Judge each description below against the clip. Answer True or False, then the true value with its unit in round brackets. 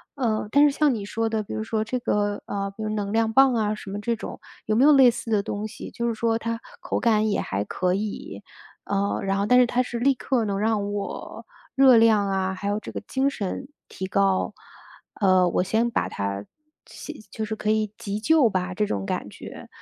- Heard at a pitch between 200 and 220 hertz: True (215 Hz)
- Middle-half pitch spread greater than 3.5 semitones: False (2.9 semitones)